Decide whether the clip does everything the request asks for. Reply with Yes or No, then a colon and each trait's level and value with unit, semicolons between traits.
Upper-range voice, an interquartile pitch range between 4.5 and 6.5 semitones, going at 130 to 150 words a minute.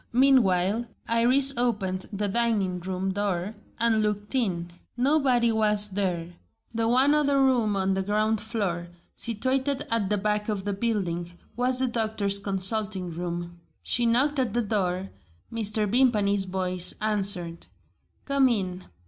No: high, 210 Hz; average, 3.9 semitones; average, 140 wpm